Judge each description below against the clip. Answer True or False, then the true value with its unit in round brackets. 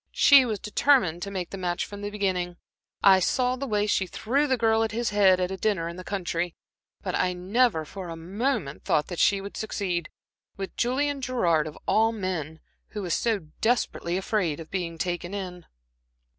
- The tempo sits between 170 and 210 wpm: True (190 wpm)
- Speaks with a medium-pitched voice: False (195 Hz)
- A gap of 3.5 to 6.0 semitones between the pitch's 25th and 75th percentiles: True (4.0 semitones)